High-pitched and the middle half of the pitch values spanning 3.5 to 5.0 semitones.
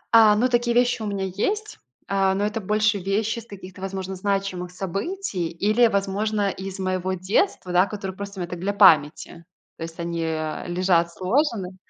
No: high, 195 Hz; average, 2.7 semitones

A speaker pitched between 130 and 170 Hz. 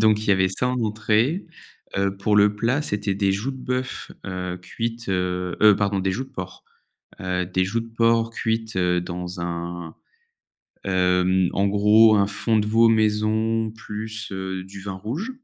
No: low, 105 Hz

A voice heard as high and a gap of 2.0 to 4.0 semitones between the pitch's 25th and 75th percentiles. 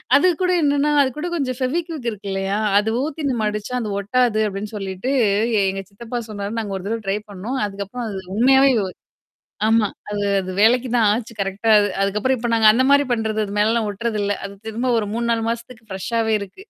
Yes: high, 225 Hz; average, 3.6 semitones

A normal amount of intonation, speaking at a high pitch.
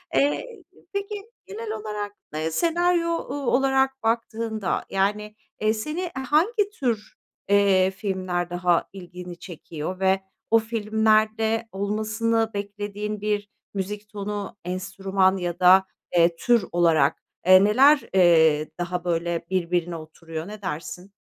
Yes: average, 3.8 semitones; high, 205 Hz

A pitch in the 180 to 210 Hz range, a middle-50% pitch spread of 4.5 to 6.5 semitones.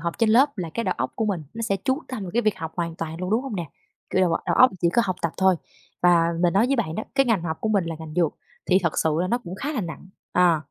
Yes: medium, 185 Hz; average, 5.1 semitones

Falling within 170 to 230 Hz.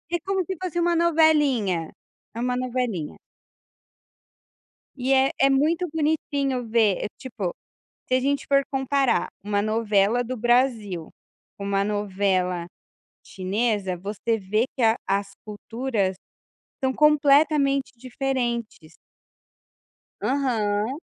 No: high, 240 Hz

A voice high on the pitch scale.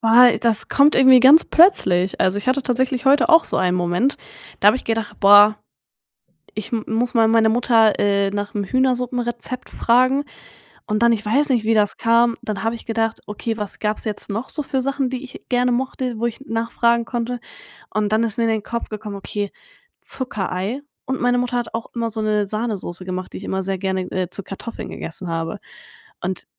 Yes: high, 225 Hz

